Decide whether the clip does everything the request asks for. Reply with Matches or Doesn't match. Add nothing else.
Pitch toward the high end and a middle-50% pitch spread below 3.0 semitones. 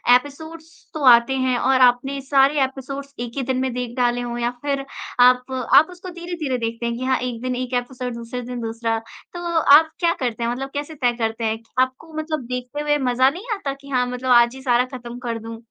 Matches